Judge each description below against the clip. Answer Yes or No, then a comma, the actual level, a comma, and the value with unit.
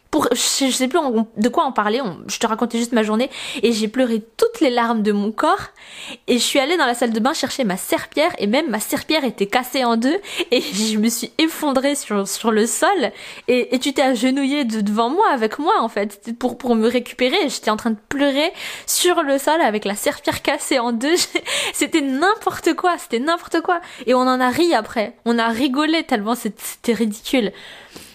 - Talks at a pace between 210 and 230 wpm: Yes, fast, 220 wpm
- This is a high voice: Yes, very high, 255 Hz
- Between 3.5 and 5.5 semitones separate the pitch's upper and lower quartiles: Yes, average, 5.2 semitones